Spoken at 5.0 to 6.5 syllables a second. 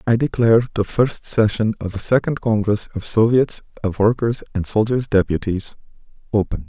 Yes: 5.2 syllables/s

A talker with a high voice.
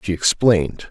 No: very low, 95 Hz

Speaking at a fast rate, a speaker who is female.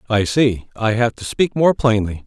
No: fast, 210 wpm; male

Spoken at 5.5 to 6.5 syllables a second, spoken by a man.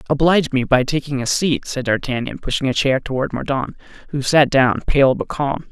No: 5.3 syllables/s; male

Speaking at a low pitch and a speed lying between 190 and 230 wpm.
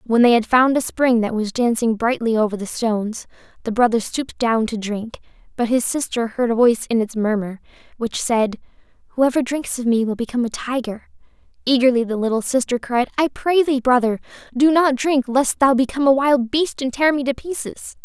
No: high, 245 Hz; fast, 205 wpm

